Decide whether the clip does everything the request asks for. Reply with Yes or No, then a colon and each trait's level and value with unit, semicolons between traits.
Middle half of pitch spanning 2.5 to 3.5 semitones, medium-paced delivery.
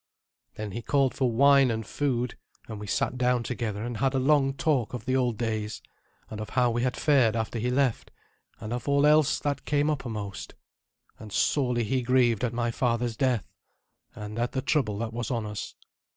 Yes: average, 3.0 semitones; average, 195 wpm